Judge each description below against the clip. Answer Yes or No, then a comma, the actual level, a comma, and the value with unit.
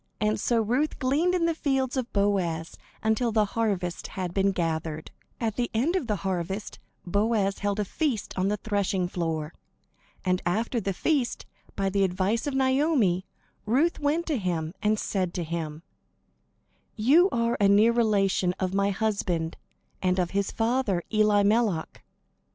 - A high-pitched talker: Yes, high, 205 Hz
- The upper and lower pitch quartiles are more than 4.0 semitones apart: Yes, average, 4.4 semitones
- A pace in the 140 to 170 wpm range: Yes, average, 155 wpm